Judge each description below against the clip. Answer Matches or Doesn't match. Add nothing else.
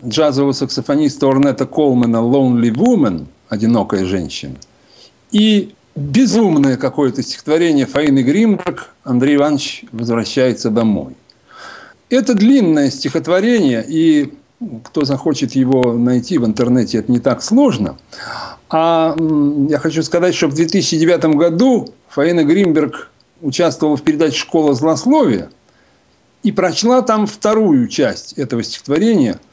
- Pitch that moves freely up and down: Matches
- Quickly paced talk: Doesn't match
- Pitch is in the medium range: Matches